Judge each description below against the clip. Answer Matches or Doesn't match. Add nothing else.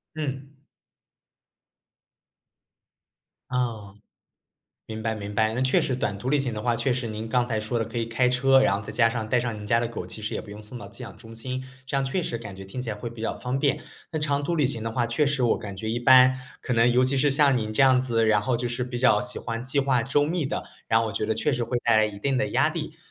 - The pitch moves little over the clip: Doesn't match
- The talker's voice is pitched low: Matches